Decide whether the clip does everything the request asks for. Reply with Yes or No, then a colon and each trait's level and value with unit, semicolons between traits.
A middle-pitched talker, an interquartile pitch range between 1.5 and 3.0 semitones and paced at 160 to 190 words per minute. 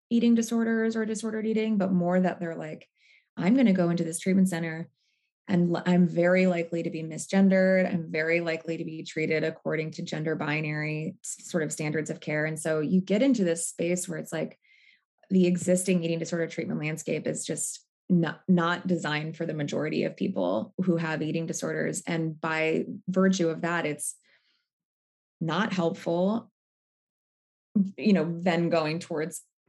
Yes: medium, 170 Hz; average, 2.7 semitones; average, 170 wpm